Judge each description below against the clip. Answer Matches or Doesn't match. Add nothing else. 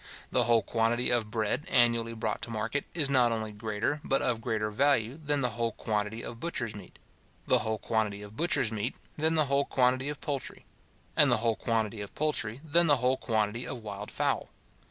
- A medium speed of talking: Matches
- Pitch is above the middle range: Doesn't match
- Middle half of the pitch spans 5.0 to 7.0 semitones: Doesn't match